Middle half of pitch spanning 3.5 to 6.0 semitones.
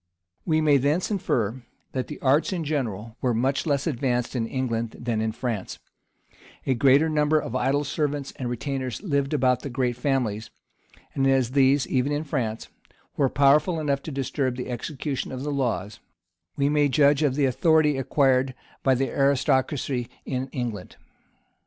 No: average, 2.7 semitones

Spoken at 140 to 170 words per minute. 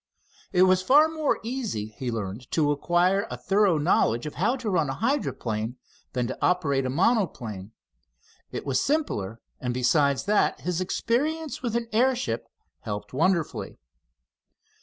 Yes: average, 150 wpm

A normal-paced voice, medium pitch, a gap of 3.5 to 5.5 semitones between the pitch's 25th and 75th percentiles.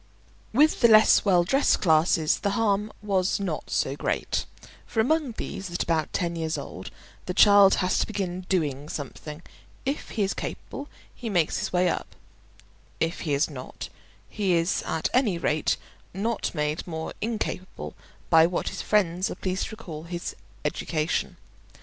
Yes: average, 160 wpm; medium, 180 Hz; average, 4.3 semitones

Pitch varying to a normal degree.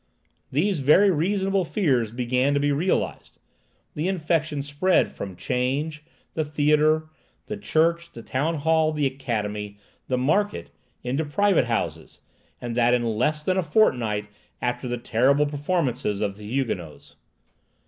Yes: average, 4.7 semitones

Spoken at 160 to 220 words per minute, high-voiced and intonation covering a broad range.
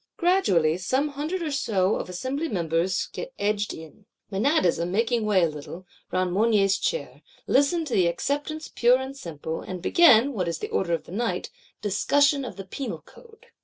Yes: average, 175 wpm; high, 215 Hz; wide, 7.8 semitones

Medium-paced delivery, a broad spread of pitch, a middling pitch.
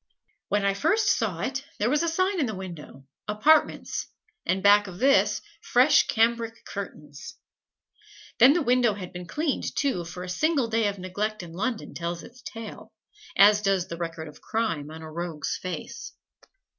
No: average, 170 wpm; wide, 6.1 semitones; high, 205 Hz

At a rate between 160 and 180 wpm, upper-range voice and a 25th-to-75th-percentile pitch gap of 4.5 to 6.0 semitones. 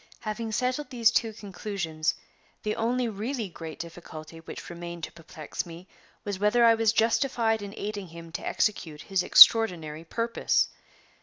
No: average, 150 wpm; high, 205 Hz; average, 5.2 semitones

